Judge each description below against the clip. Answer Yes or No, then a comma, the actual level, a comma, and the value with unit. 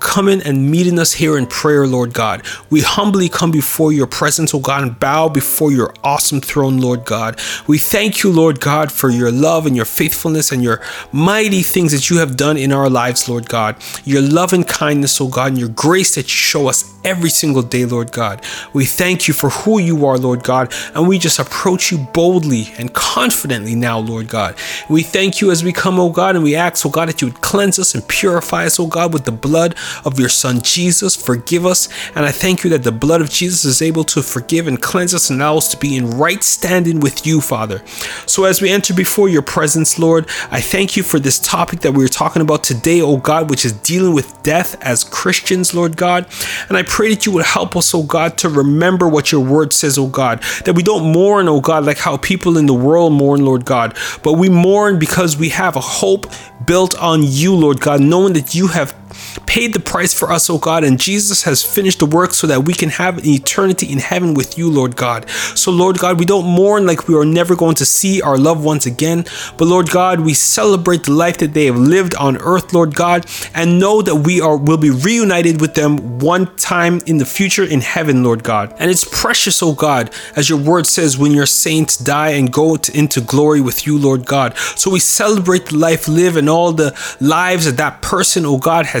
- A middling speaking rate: No, fast, 235 wpm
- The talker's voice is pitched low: No, medium, 160 Hz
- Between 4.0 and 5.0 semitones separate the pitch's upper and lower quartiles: Yes, average, 4.5 semitones